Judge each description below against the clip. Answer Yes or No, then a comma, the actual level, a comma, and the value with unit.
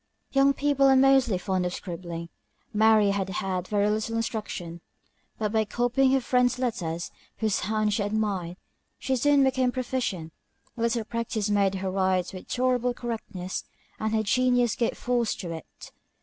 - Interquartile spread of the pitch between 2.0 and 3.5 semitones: No, average, 4.7 semitones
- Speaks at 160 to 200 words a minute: Yes, average, 165 wpm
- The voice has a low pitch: No, high, 220 Hz